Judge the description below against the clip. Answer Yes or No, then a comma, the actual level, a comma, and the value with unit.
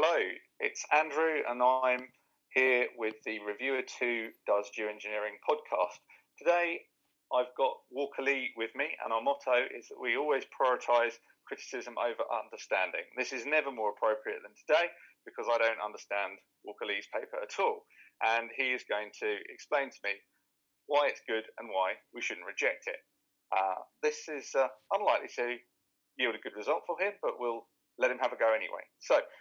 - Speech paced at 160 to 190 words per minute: Yes, average, 175 wpm